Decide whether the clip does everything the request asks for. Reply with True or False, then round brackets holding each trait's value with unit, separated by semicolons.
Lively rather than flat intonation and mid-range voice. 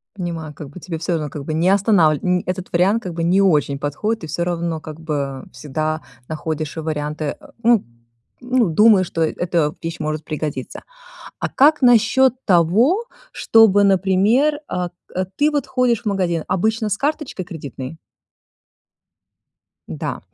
True (5.8 semitones; 175 Hz)